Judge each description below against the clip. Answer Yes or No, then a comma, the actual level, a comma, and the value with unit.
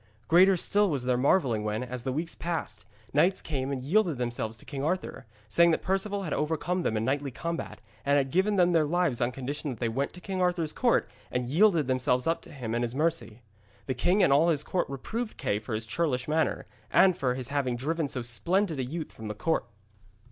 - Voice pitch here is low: No, medium, 145 Hz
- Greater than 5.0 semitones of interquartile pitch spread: Yes, wide, 5.6 semitones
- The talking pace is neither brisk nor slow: No, fast, 220 wpm